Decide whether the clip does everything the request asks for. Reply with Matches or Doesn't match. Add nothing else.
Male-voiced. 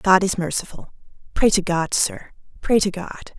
Doesn't match